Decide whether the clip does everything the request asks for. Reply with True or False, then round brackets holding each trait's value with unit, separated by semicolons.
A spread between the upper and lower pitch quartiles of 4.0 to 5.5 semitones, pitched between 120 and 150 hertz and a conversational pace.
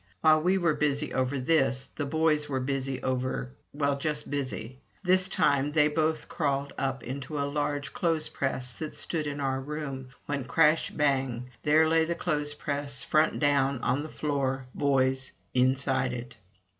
False (2.5 semitones; 140 Hz; 160 wpm)